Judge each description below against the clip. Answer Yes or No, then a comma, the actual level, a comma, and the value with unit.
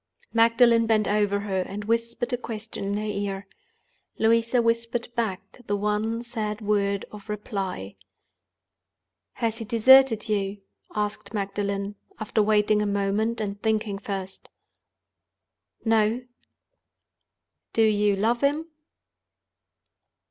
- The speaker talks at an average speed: No, slow, 110 wpm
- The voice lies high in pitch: Yes, high, 210 Hz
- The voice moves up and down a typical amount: No, narrow, 2.2 semitones